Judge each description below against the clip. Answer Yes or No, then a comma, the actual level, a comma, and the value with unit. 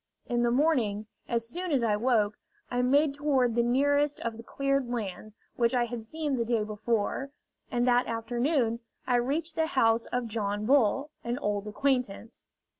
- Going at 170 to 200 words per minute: Yes, average, 175 wpm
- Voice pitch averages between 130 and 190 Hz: No, high, 240 Hz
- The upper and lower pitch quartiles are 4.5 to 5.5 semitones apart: No, average, 3.5 semitones